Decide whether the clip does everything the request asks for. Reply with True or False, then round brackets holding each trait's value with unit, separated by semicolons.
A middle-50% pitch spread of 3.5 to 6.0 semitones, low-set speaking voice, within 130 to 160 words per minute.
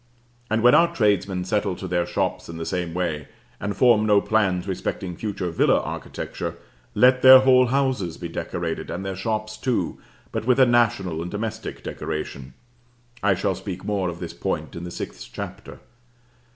False (4.1 semitones; 100 Hz; 175 wpm)